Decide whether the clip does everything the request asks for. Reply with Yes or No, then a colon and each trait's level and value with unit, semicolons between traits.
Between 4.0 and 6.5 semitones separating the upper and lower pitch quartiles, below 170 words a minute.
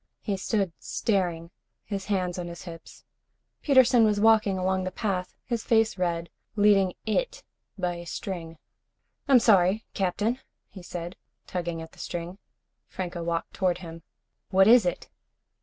No: average, 3.4 semitones; average, 145 wpm